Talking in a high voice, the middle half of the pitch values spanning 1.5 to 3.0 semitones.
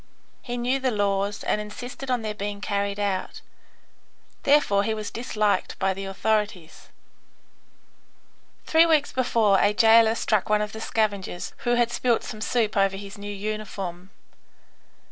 Yes: high, 210 Hz; narrow, 2.6 semitones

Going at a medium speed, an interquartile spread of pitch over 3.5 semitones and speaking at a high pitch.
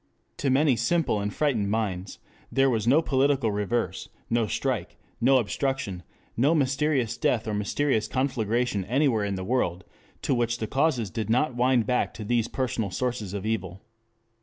No: average, 160 wpm; average, 4.3 semitones; low, 120 Hz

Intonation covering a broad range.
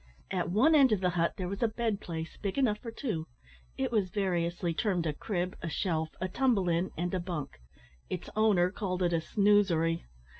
No: average, 3.6 semitones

